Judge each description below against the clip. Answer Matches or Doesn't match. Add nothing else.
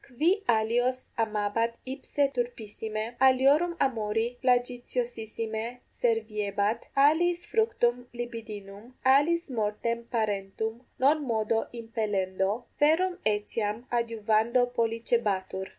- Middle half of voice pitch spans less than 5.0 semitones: Matches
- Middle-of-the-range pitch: Doesn't match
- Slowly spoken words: Matches